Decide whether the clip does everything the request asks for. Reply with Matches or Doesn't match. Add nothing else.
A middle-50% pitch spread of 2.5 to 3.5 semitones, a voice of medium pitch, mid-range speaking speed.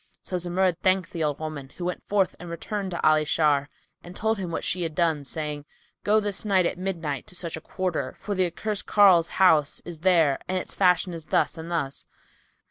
Doesn't match